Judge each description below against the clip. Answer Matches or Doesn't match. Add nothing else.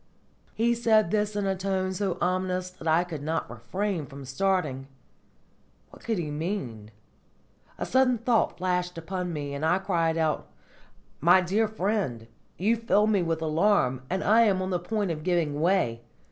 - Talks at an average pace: Matches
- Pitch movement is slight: Doesn't match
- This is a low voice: Doesn't match